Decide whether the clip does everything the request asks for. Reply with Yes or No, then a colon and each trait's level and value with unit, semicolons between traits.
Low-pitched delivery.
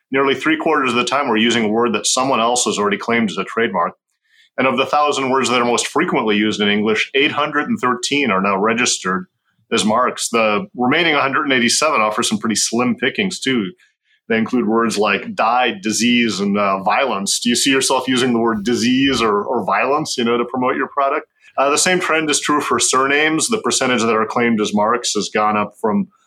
Yes: low, 120 Hz